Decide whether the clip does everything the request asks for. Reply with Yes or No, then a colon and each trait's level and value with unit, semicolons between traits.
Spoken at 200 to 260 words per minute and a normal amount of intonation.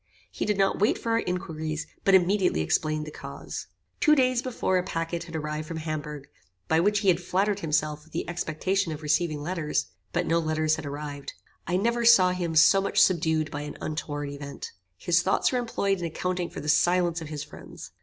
Yes: fast, 205 wpm; average, 3.6 semitones